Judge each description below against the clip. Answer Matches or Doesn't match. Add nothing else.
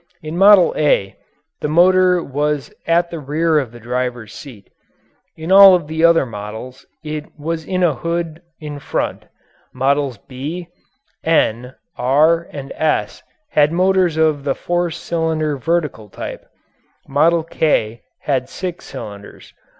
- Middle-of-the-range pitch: Matches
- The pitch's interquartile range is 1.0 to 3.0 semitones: Doesn't match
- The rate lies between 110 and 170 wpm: Matches